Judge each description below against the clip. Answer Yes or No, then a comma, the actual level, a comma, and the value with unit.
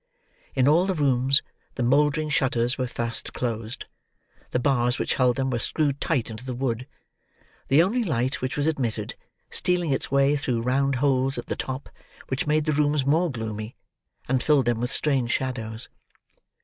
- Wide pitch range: No, average, 3.1 semitones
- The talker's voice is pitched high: No, low, 130 Hz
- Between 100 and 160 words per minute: No, average, 175 wpm